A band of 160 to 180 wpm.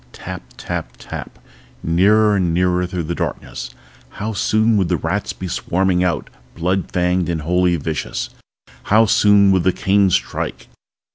No: average, 150 wpm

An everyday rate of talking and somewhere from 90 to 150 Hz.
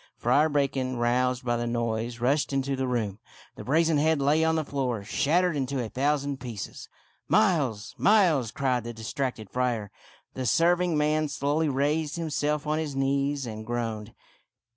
Yes: average, 170 wpm; low, 135 Hz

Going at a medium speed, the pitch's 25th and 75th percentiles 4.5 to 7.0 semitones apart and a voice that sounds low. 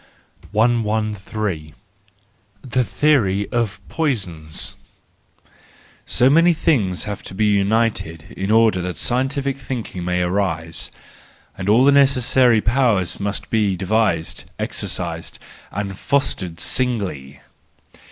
No: slow, 105 wpm; average, 5.2 semitones; low, 105 Hz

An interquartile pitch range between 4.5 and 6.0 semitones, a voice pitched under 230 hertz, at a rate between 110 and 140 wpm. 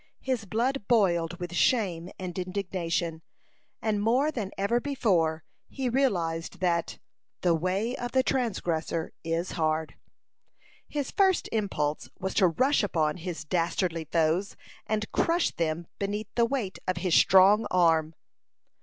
Yes: wide, 5.4 semitones; medium, 185 Hz; slow, 135 wpm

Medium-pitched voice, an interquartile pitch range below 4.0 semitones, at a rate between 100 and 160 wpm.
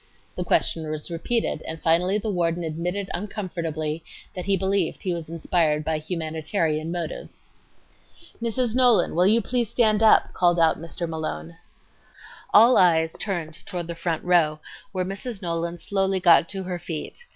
Yes: medium, 175 Hz; average, 3.4 semitones; average, 155 wpm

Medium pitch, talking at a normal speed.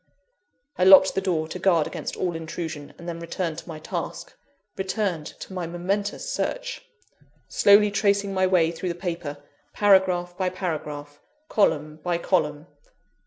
Yes: medium, 175 Hz; average, 150 wpm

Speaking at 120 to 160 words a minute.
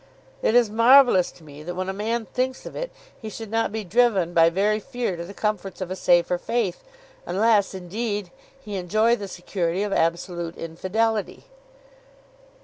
No: average, 170 wpm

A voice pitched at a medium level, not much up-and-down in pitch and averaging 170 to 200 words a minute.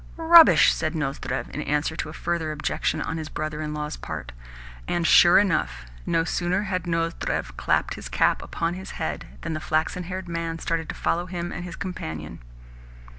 Yes: medium, 165 Hz; narrow, 2.3 semitones; average, 180 wpm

